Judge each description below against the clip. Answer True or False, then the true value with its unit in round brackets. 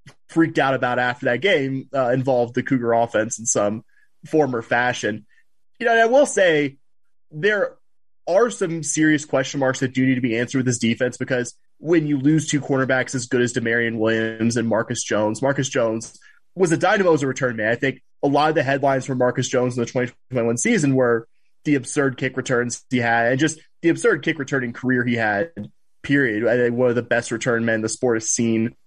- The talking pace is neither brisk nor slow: False (215 wpm)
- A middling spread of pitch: True (3.5 semitones)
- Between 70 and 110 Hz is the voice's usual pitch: False (130 Hz)